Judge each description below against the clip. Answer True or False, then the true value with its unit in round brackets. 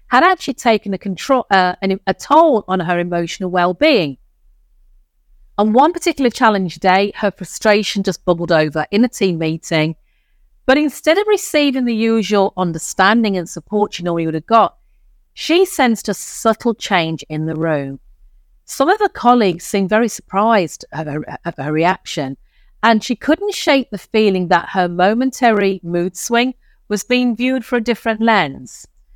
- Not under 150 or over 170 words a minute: True (160 wpm)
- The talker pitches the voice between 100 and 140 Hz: False (200 Hz)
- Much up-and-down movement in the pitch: True (5.7 semitones)